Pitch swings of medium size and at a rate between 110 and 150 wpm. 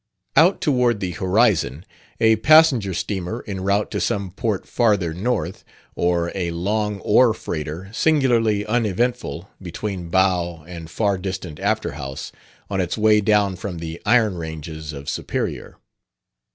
Yes: average, 4.2 semitones; slow, 135 wpm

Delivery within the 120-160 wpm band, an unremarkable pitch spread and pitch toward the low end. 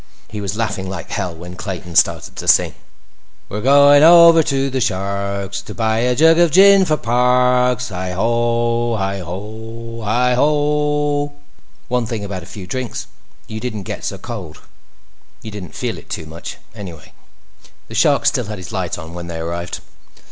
No: average, 170 wpm; average, 4.9 semitones; low, 110 Hz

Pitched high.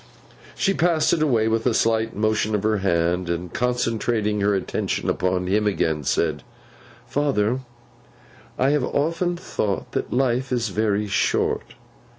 No: low, 110 Hz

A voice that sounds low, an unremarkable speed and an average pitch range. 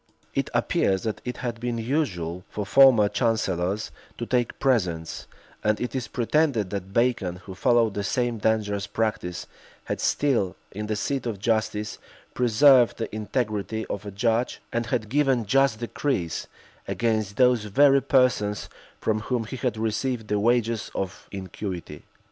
Yes: low, 110 Hz; average, 150 wpm; average, 3.3 semitones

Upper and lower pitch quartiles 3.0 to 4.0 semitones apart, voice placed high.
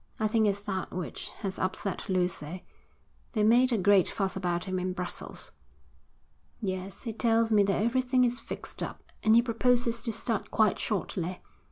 Yes: average, 3.7 semitones; high, 205 Hz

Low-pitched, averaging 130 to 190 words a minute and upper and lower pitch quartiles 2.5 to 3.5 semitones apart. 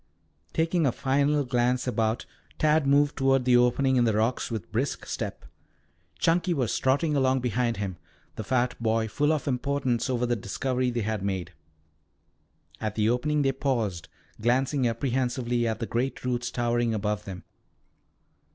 Yes: low, 125 Hz; average, 155 wpm; average, 3.0 semitones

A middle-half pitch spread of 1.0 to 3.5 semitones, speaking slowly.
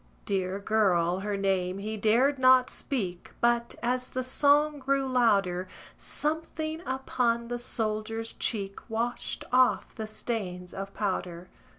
No: average, 4.6 semitones; slow, 125 wpm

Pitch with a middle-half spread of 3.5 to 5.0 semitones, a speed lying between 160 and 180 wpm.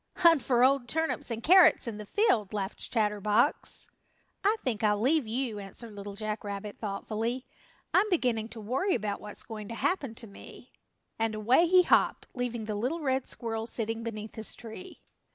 Yes: average, 4.1 semitones; average, 175 wpm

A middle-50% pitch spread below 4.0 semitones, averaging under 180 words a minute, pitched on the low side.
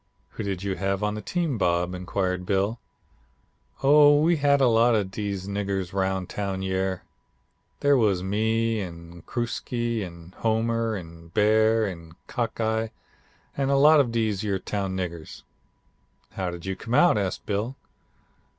Yes: average, 3.5 semitones; average, 150 wpm; low, 105 Hz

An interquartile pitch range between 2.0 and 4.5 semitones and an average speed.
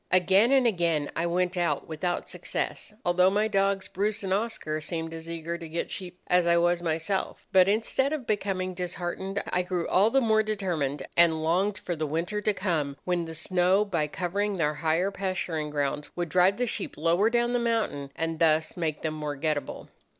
Yes: average, 3.5 semitones; average, 195 wpm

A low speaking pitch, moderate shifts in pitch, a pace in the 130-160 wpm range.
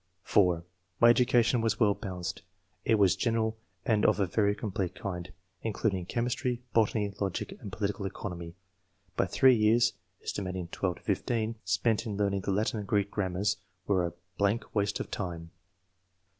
Yes: low, 100 Hz; average, 3.0 semitones; average, 155 wpm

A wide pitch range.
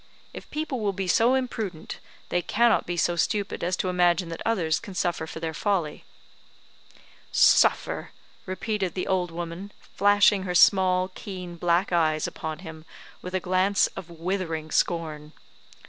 No: average, 2.9 semitones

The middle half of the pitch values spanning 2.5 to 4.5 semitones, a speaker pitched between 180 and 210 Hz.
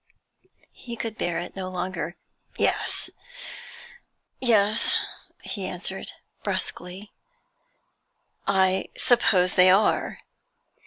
Yes: average, 2.9 semitones; high, 190 Hz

